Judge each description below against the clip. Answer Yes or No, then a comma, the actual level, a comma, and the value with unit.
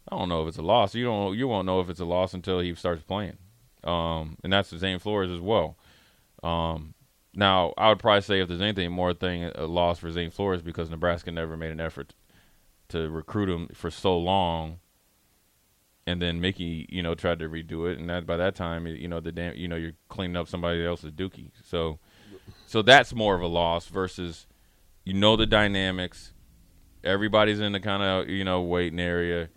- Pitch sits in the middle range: No, very low, 90 Hz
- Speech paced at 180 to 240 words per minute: Yes, fast, 205 wpm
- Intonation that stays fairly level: Yes, narrow, 2.3 semitones